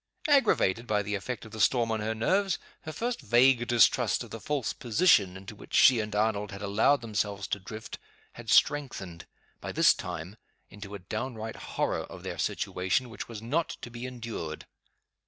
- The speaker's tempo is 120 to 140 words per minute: No, average, 180 wpm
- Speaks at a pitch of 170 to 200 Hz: No, low, 110 Hz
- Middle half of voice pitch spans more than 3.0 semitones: Yes, average, 3.5 semitones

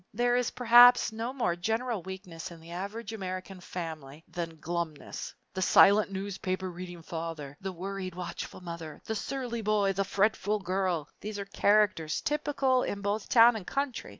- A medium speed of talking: Yes, average, 160 wpm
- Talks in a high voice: Yes, high, 195 Hz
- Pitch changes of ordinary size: Yes, average, 4.2 semitones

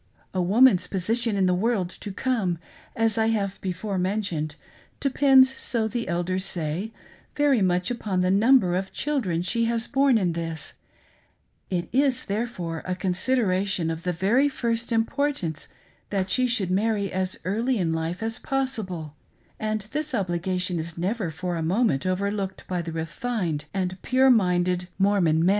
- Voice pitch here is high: Yes, high, 195 Hz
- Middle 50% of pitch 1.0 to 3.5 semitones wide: No, average, 4.6 semitones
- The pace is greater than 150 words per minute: Yes, average, 160 wpm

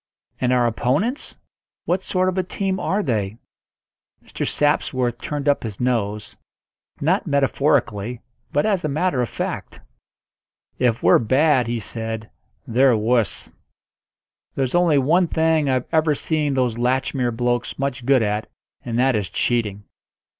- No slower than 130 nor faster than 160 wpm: Yes, average, 140 wpm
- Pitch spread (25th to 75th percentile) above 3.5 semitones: Yes, average, 4.5 semitones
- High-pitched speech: No, low, 130 Hz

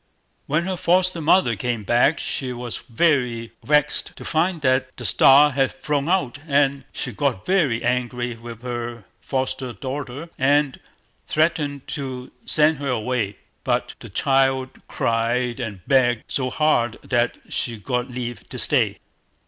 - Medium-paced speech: Yes, average, 145 wpm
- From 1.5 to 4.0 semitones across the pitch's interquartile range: Yes, average, 3.2 semitones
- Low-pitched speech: Yes, low, 130 Hz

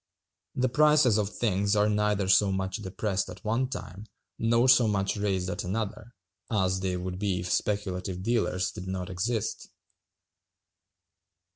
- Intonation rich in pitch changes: No, average, 2.9 semitones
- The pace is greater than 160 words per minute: No, average, 145 wpm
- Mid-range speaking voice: No, low, 100 Hz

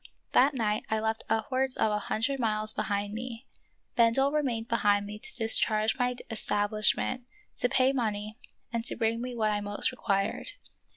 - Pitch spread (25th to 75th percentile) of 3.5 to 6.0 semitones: No, average, 2.8 semitones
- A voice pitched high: Yes, high, 225 Hz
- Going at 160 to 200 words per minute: Yes, average, 170 wpm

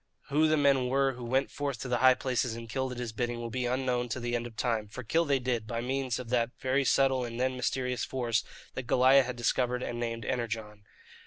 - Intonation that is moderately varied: No, narrow, 1.9 semitones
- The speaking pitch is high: No, low, 125 Hz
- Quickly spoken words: Yes, fast, 240 wpm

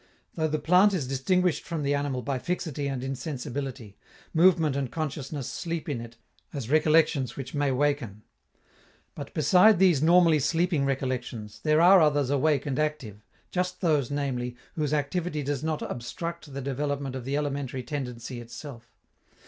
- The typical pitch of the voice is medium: Yes, medium, 145 Hz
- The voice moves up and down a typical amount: Yes, average, 3.3 semitones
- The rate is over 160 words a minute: No, average, 155 wpm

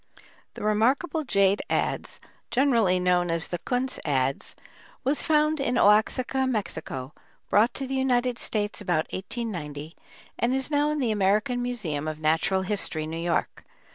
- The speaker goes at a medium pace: Yes, average, 150 wpm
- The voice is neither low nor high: No, high, 215 Hz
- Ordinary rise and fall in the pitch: No, wide, 6.8 semitones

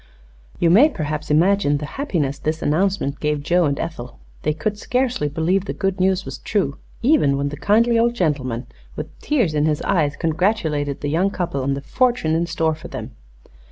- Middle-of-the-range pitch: Yes, medium, 160 Hz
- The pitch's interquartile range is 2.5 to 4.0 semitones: No, average, 5.3 semitones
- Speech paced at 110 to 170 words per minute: No, average, 190 wpm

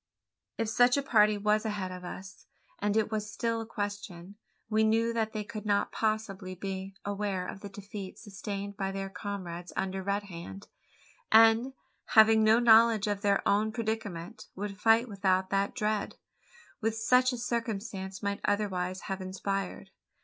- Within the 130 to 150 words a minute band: No, average, 160 wpm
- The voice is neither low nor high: No, high, 205 Hz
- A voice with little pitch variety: Yes, narrow, 2.3 semitones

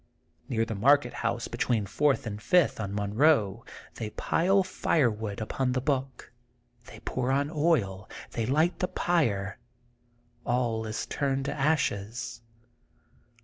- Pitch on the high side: No, low, 125 Hz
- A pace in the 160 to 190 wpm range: No, slow, 135 wpm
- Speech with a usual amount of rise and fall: Yes, average, 4.9 semitones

